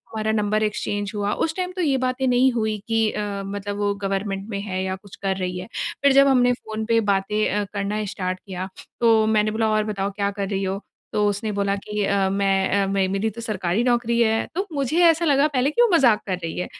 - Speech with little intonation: No, average, 3.2 semitones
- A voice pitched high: Yes, high, 210 Hz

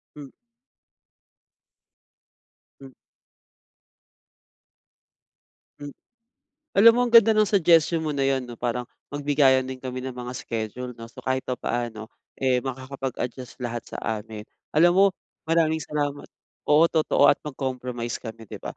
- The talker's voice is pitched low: Yes, low, 130 Hz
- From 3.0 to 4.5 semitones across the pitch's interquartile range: Yes, average, 3.5 semitones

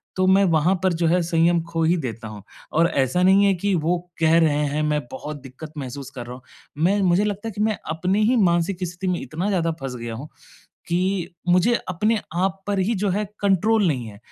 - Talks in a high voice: No, medium, 175 Hz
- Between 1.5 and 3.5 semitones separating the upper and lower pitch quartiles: No, average, 4.2 semitones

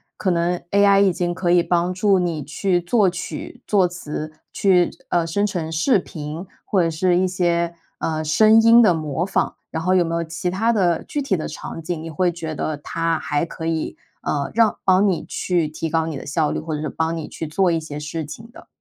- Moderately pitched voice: Yes, medium, 170 Hz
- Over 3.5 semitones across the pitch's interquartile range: No, average, 2.7 semitones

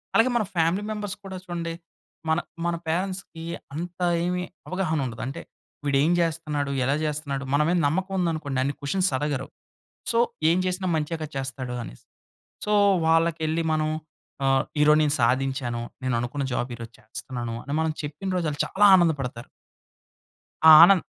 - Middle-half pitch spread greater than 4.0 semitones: Yes, average, 4.4 semitones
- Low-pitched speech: No, medium, 155 Hz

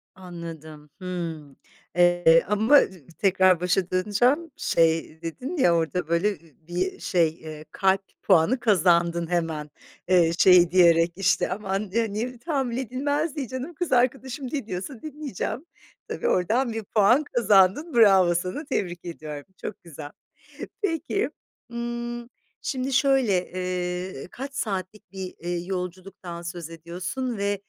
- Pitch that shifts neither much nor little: No, wide, 5.9 semitones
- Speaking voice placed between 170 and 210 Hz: Yes, high, 190 Hz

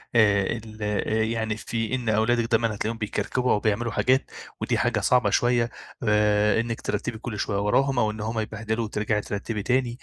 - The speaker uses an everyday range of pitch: No, narrow, 1.9 semitones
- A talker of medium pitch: No, low, 110 Hz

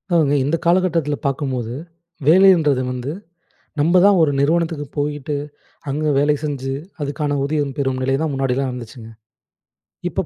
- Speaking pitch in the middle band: Yes, medium, 145 Hz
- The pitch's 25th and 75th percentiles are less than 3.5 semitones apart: Yes, average, 2.8 semitones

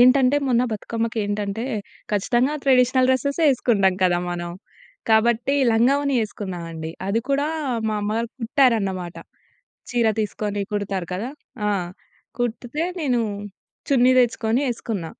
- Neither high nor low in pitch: No, high, 230 Hz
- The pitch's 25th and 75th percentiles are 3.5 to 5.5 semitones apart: Yes, average, 3.8 semitones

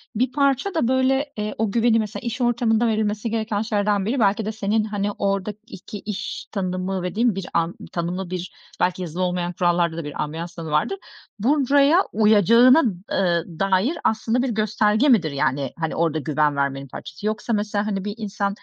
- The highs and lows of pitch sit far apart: No, average, 4.1 semitones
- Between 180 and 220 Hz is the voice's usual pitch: Yes, high, 205 Hz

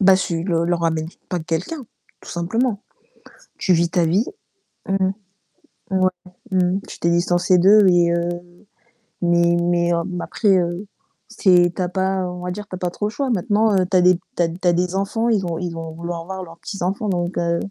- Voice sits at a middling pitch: Yes, medium, 180 Hz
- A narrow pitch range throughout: Yes, narrow, 2.0 semitones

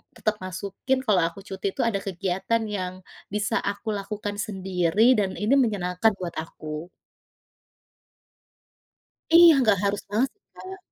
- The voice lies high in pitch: Yes, high, 200 Hz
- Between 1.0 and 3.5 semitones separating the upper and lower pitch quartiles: Yes, average, 2.9 semitones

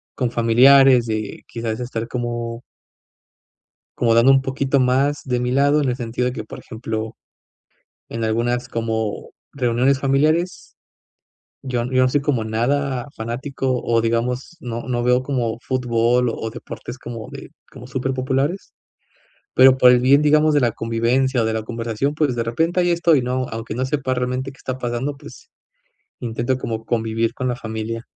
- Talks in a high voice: No, low, 125 Hz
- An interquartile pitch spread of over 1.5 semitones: Yes, narrow, 2.5 semitones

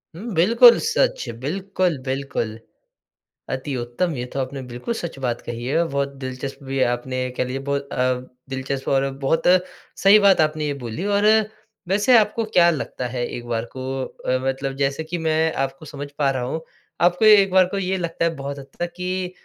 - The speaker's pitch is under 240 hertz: Yes, medium, 140 Hz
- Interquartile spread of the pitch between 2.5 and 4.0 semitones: No, wide, 5.6 semitones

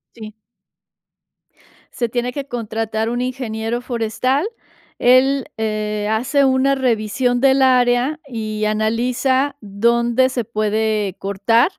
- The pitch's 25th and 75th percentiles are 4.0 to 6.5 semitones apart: No, average, 3.0 semitones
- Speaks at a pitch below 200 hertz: No, high, 235 Hz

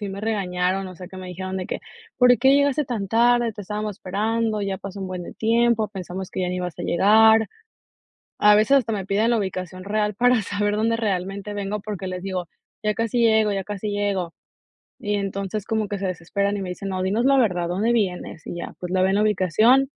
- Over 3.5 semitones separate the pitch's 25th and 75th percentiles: No, average, 2.8 semitones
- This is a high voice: Yes, high, 205 Hz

